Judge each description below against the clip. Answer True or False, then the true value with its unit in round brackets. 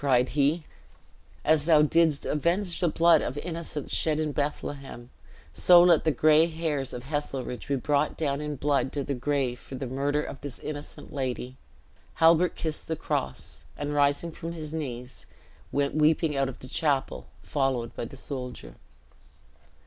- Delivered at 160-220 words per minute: True (165 wpm)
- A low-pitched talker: False (145 Hz)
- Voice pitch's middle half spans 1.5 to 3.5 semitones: True (2.7 semitones)